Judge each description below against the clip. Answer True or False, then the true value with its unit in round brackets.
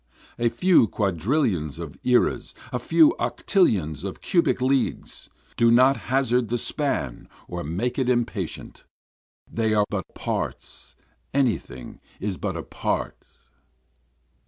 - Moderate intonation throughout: False (6.0 semitones)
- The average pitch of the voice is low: True (115 Hz)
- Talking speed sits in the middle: False (125 wpm)